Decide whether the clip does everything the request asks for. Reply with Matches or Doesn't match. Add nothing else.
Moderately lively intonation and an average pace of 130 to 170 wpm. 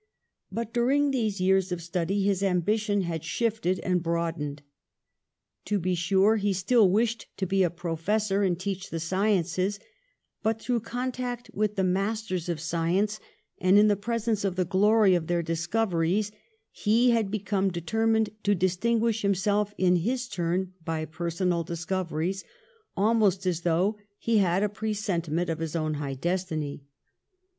Matches